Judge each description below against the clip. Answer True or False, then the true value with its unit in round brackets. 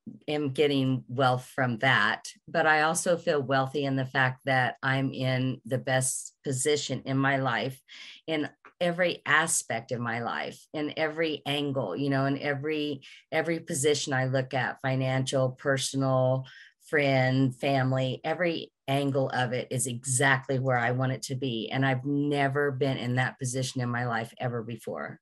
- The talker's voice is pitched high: False (135 Hz)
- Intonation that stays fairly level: True (2.0 semitones)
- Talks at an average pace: True (160 wpm)